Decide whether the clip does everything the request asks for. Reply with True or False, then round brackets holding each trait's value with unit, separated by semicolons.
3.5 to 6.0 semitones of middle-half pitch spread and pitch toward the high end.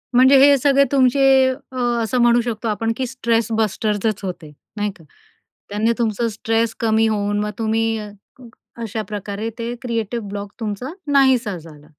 False (2.5 semitones; 225 Hz)